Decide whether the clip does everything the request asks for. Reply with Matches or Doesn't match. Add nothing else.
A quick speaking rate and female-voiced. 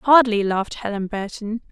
Doesn't match